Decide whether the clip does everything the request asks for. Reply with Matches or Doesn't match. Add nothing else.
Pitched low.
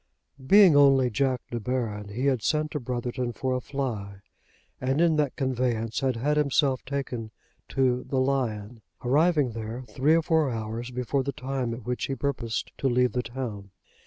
Matches